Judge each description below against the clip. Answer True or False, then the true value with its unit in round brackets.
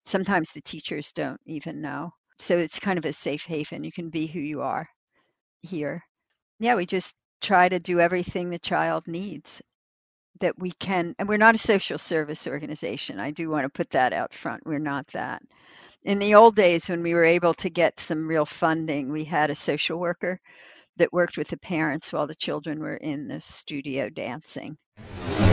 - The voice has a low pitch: False (165 Hz)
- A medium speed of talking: True (195 wpm)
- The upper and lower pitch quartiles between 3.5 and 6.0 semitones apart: False (2.9 semitones)